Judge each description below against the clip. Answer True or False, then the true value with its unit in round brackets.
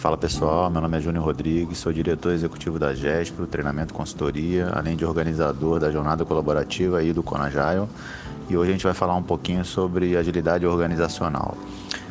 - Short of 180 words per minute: True (170 wpm)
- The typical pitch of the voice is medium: False (85 Hz)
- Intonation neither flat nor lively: False (1.9 semitones)